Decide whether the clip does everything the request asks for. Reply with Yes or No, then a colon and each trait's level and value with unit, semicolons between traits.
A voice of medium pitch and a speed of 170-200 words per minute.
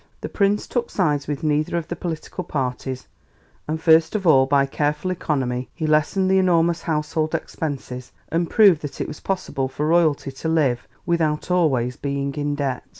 Yes: medium, 155 Hz; average, 175 wpm